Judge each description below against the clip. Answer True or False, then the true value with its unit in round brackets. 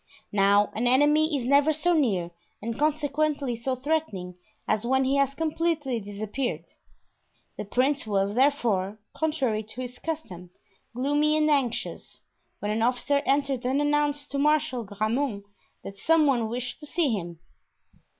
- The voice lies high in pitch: True (265 Hz)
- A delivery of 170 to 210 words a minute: False (150 wpm)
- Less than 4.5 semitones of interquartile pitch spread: False (5.3 semitones)